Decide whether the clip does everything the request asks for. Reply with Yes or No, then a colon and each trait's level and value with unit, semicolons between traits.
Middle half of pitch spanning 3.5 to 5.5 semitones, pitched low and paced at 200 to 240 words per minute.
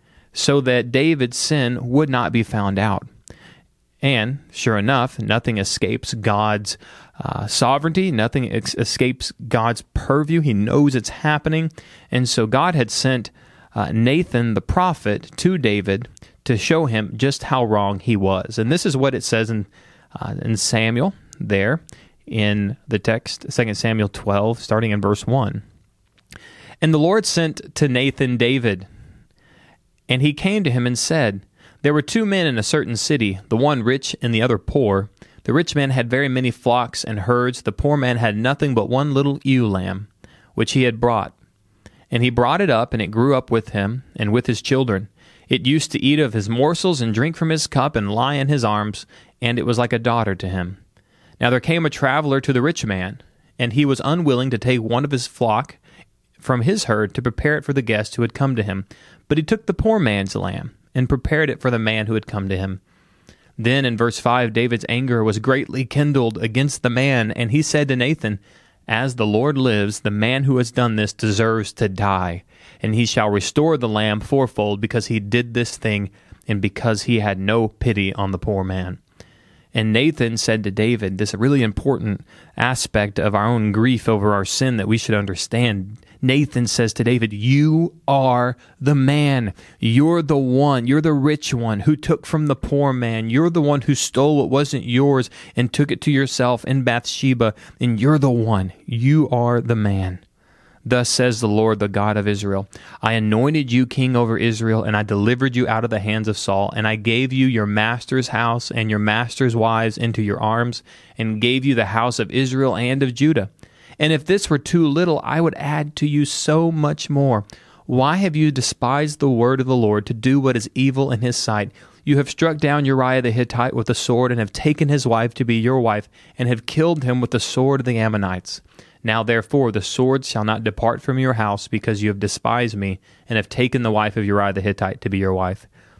Yes: average, 4.1 semitones; low, 120 Hz; fast, 205 wpm